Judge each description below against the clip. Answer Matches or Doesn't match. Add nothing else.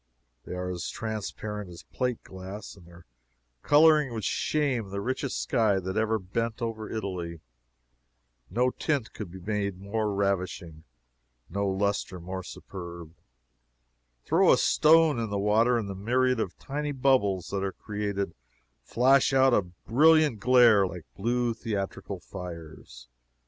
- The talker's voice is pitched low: Matches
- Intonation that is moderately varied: Matches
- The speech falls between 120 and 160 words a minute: Matches